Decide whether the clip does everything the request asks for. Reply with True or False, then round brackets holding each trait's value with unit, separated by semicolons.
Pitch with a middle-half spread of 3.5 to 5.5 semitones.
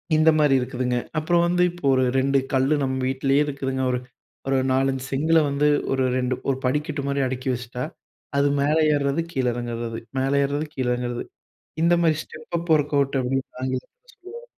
False (2.9 semitones)